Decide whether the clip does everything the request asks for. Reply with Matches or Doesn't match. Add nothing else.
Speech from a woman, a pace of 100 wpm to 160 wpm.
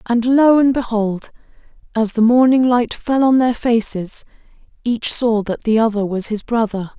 Doesn't match